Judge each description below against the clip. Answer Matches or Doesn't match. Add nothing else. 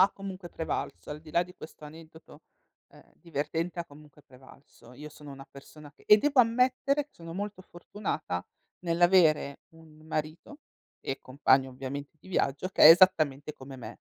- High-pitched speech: Doesn't match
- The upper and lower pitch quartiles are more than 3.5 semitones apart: Matches